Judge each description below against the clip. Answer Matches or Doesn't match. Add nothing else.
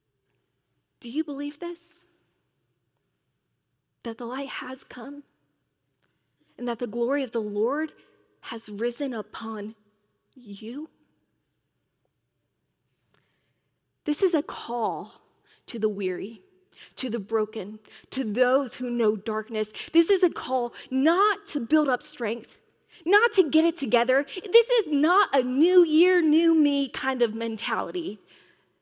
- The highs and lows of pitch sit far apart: Matches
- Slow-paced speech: Matches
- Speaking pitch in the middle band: Doesn't match